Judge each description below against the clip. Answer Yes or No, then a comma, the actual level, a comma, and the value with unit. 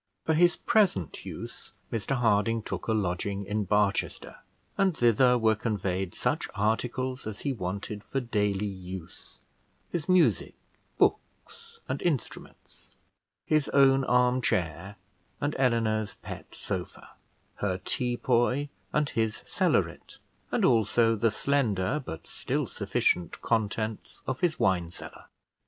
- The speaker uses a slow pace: Yes, slow, 125 wpm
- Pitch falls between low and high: No, low, 115 Hz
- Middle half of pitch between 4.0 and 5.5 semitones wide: Yes, average, 4.6 semitones